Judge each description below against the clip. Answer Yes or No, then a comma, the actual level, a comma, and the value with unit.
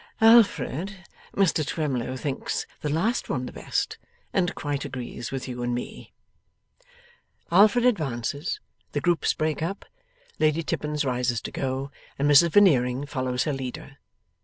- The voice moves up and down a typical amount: Yes, average, 5.0 semitones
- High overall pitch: No, medium, 145 Hz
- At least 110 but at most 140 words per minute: Yes, slow, 135 wpm